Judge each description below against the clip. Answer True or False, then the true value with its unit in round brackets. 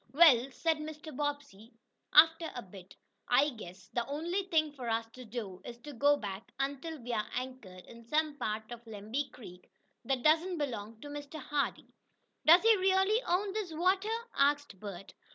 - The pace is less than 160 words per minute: False (170 wpm)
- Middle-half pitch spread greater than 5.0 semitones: True (5.6 semitones)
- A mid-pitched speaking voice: False (280 Hz)